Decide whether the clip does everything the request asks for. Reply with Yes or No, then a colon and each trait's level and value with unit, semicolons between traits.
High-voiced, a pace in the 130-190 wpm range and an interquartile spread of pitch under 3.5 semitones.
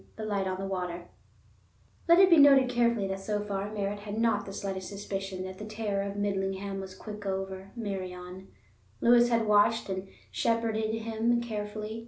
Yes: high, 205 Hz; average, 175 wpm; narrow, 2.6 semitones